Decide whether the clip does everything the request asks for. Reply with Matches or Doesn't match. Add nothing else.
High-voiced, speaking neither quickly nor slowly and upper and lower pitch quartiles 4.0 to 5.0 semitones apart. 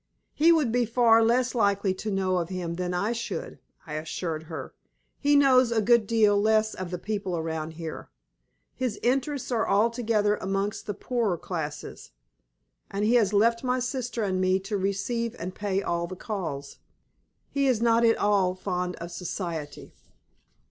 Matches